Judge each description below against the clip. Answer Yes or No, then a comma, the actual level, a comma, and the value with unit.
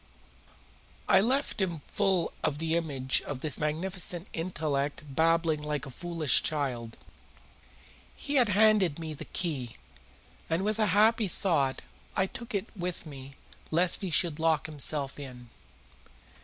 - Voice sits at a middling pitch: Yes, medium, 165 Hz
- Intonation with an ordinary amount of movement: Yes, average, 4.5 semitones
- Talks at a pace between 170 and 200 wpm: No, average, 140 wpm